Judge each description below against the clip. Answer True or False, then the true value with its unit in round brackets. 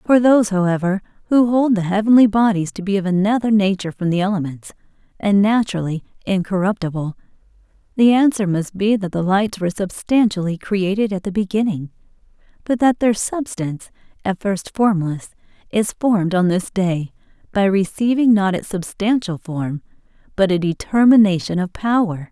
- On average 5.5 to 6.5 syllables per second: False (5.3 syllables/s)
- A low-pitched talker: False (200 Hz)